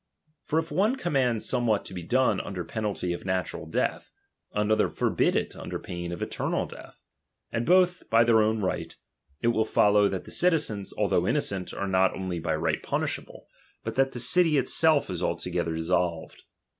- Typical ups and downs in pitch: No, wide, 6.3 semitones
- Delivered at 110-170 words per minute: No, average, 180 wpm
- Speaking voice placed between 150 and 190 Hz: No, low, 110 Hz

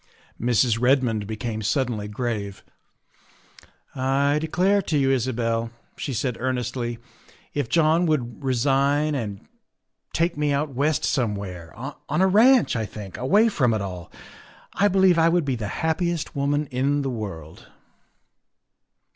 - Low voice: Yes, low, 130 Hz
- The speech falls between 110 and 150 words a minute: Yes, average, 140 wpm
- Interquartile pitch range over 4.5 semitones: Yes, average, 5.0 semitones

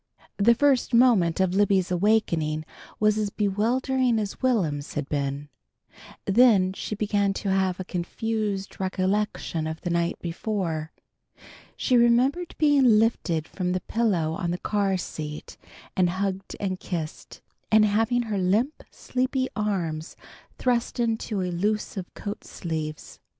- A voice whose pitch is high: Yes, high, 200 Hz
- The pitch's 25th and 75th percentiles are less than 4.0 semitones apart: No, average, 4.3 semitones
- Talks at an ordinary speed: No, slow, 130 wpm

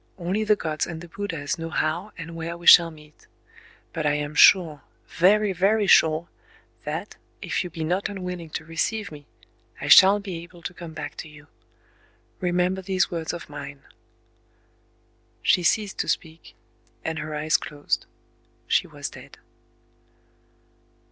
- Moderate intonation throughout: Yes, average, 3.1 semitones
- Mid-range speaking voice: Yes, medium, 170 Hz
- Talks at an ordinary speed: Yes, average, 150 wpm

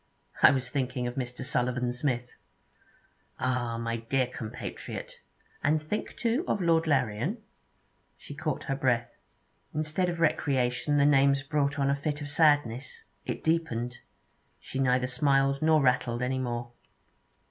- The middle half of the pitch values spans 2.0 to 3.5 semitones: Yes, average, 3.0 semitones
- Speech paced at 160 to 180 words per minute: No, average, 140 wpm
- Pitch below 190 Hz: Yes, low, 135 Hz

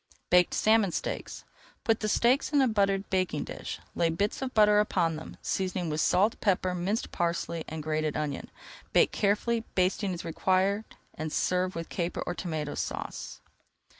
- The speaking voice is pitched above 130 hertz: Yes, medium, 185 Hz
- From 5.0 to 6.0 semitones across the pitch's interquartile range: No, average, 3.8 semitones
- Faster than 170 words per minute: No, average, 165 wpm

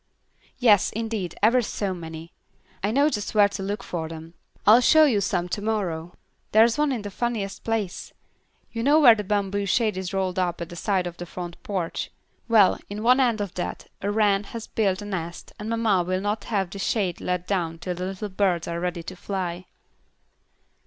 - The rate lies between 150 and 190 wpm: No, average, 200 wpm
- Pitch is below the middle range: No, high, 200 Hz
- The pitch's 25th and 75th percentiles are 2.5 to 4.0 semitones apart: Yes, average, 3.5 semitones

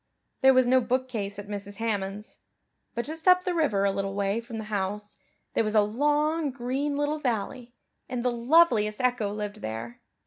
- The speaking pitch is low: No, high, 235 Hz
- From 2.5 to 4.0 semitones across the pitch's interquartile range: No, average, 4.5 semitones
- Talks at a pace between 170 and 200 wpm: Yes, average, 180 wpm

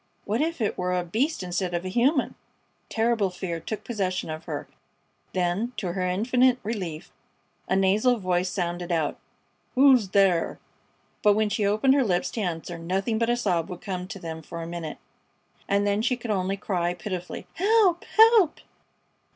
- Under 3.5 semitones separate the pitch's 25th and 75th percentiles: No, average, 4.9 semitones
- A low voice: No, high, 195 Hz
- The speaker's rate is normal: Yes, average, 175 wpm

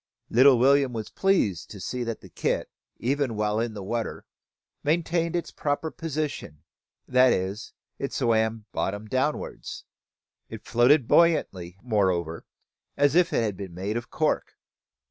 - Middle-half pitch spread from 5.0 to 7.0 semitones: Yes, wide, 5.6 semitones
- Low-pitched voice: Yes, low, 120 Hz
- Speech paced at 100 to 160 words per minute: Yes, average, 145 wpm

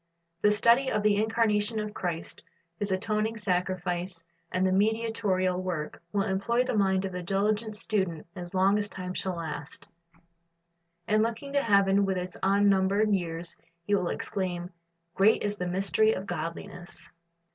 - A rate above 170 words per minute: No, average, 150 wpm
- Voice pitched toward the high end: Yes, high, 195 Hz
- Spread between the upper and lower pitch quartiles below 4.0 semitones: Yes, average, 2.7 semitones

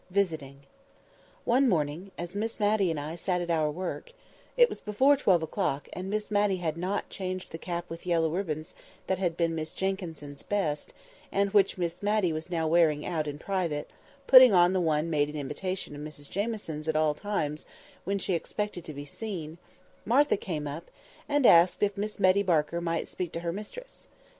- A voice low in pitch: No, medium, 175 Hz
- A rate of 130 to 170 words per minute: No, average, 185 wpm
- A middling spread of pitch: Yes, average, 4.3 semitones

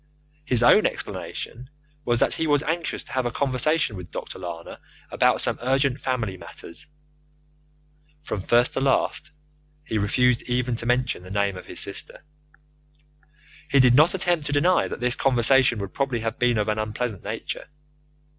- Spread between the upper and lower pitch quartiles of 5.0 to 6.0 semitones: No, average, 4.1 semitones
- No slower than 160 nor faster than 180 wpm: Yes, average, 165 wpm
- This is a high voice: No, low, 125 Hz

